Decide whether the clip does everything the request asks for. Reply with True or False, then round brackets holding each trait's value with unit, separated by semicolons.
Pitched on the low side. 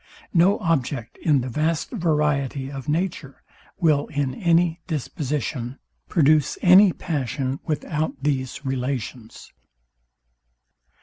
False (150 Hz)